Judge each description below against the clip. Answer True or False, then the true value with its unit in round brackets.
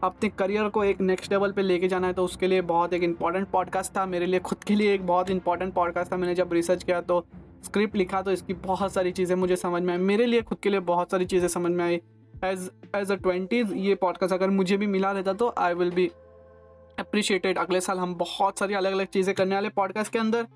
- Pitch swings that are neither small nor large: False (1.8 semitones)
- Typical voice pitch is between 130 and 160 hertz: False (185 Hz)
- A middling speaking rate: False (245 wpm)